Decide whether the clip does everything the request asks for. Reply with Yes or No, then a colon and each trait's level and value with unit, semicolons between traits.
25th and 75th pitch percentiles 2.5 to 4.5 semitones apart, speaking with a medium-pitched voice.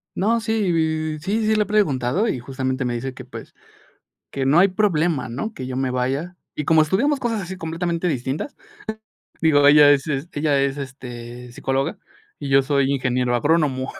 No: average, 5.1 semitones; medium, 145 Hz